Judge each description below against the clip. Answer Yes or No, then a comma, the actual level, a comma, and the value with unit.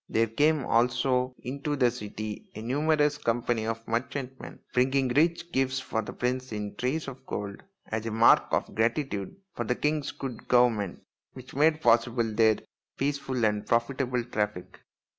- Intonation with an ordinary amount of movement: Yes, average, 3.3 semitones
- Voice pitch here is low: Yes, low, 125 Hz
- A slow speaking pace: No, average, 155 wpm